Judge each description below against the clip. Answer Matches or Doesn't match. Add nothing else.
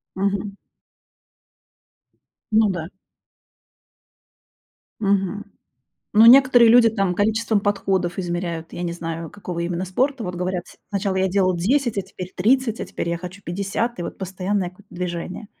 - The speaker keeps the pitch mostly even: Doesn't match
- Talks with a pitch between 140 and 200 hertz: Matches